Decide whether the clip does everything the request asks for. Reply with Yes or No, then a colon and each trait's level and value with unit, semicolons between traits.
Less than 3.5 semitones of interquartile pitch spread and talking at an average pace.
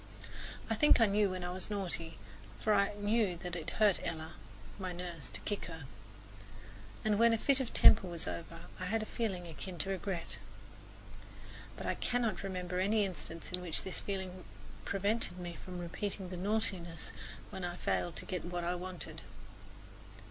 Yes: average, 2.9 semitones; average, 175 wpm